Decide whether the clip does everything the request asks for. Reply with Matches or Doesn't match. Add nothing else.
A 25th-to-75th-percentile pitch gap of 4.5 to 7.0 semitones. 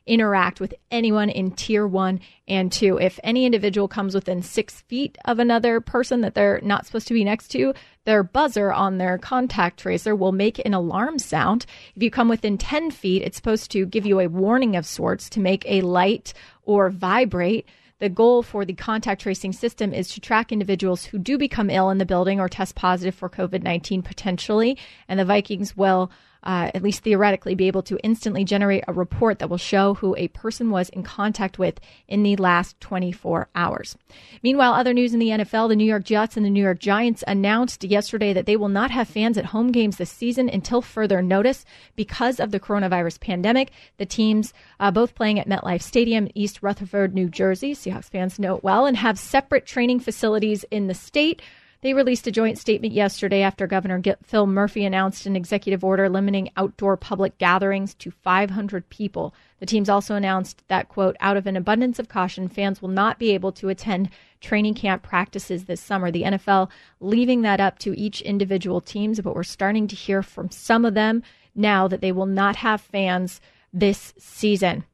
Doesn't match